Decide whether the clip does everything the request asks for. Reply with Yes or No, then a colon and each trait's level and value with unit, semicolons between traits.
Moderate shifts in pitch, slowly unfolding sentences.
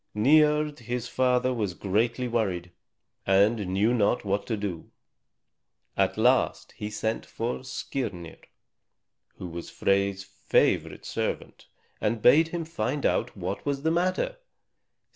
Yes: average, 5.0 semitones; slow, 125 wpm